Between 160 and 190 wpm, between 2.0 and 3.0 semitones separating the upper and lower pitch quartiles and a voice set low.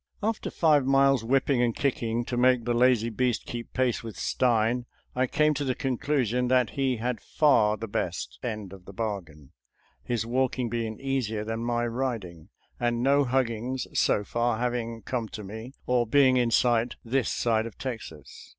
Yes: average, 180 wpm; narrow, 2.5 semitones; low, 120 Hz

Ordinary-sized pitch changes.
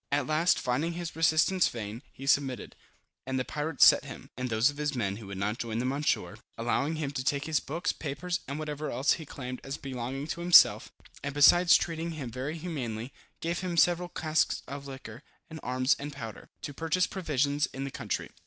Yes: average, 4.0 semitones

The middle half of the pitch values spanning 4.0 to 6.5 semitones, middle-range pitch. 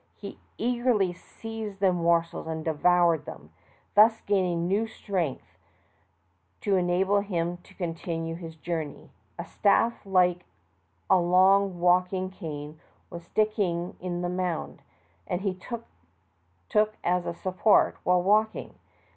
No: average, 2.7 semitones; medium, 180 Hz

